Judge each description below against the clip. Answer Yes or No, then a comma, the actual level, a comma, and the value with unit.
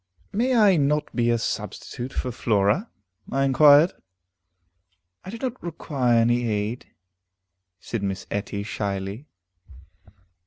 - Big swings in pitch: Yes, wide, 6.5 semitones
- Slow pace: Yes, slow, 115 wpm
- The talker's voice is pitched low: Yes, low, 125 Hz